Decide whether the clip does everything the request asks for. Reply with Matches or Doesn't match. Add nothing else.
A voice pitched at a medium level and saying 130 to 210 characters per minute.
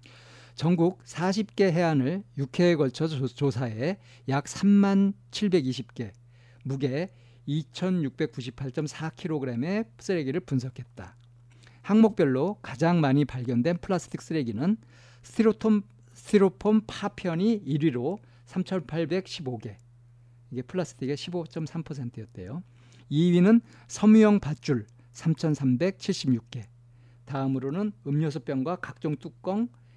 Matches